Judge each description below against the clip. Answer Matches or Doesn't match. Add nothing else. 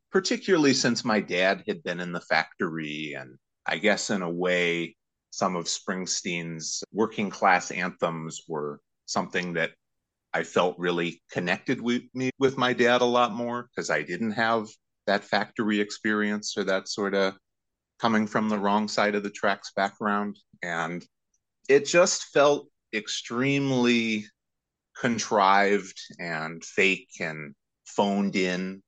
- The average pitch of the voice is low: Matches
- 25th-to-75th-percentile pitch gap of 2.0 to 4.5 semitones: Doesn't match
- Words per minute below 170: Matches